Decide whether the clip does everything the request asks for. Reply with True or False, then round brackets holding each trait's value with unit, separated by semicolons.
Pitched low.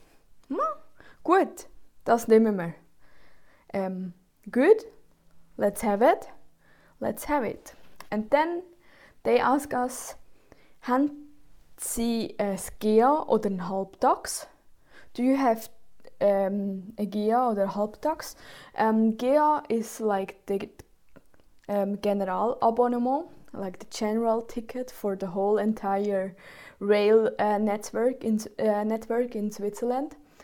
False (225 Hz)